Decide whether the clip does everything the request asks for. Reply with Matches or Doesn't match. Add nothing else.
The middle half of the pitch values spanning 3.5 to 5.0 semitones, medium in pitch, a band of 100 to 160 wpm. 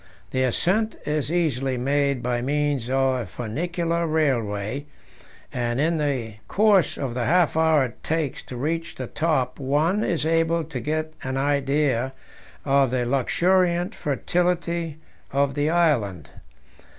Matches